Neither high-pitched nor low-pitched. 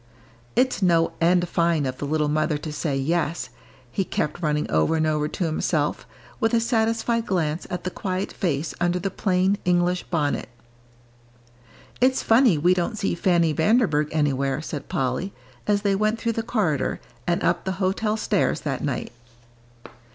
Yes: medium, 175 Hz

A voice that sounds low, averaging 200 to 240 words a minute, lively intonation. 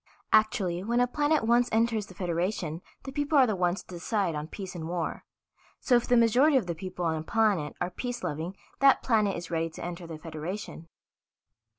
No: high, 190 Hz; fast, 205 wpm; wide, 5.7 semitones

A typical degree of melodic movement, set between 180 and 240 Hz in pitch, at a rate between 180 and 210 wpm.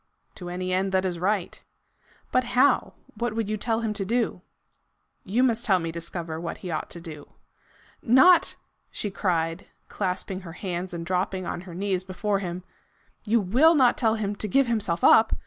Yes: average, 4.0 semitones; high, 190 Hz; average, 195 wpm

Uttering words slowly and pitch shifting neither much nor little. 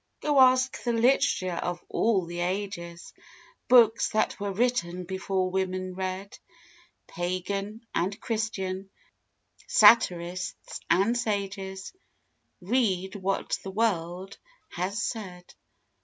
Yes: slow, 100 wpm; average, 3.3 semitones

